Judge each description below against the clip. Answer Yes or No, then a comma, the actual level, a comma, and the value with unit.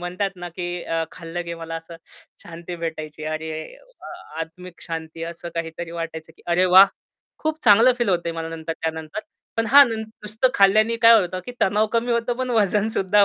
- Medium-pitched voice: Yes, medium, 175 Hz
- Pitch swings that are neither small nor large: Yes, average, 4.6 semitones